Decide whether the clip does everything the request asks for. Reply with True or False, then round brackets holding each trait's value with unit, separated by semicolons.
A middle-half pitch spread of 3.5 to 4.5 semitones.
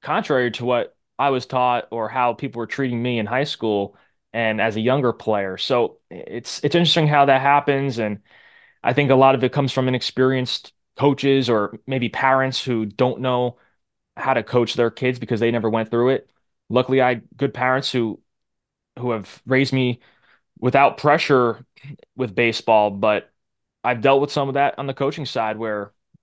False (2.8 semitones)